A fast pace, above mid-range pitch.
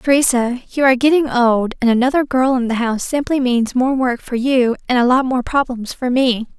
Yes: fast, 220 wpm; very high, 250 Hz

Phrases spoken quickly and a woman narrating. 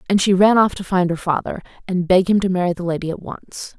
Yes: fast, 270 wpm; female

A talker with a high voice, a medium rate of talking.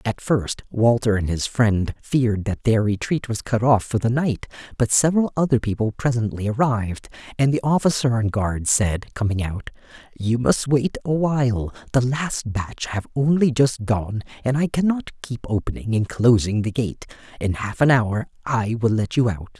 No: low, 120 Hz; average, 185 wpm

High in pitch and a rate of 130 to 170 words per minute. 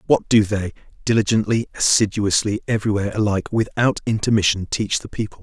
No: low, 105 Hz; slow, 135 wpm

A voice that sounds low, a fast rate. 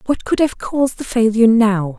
No: high, 225 Hz; fast, 210 wpm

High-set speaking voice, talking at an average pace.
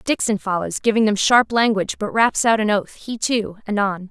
No: high, 210 Hz; fast, 220 wpm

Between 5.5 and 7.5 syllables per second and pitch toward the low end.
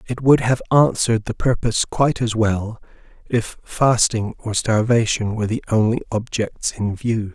No: 4.7 syllables/s; low, 115 Hz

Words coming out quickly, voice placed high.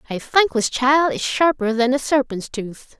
No: average, 180 wpm; very high, 260 Hz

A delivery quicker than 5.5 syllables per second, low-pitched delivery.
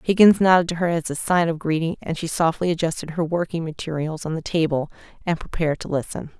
No: 6.2 syllables/s; medium, 165 Hz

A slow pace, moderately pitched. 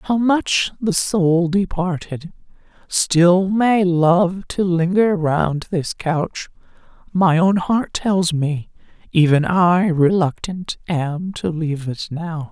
Yes: slow, 125 wpm; medium, 175 Hz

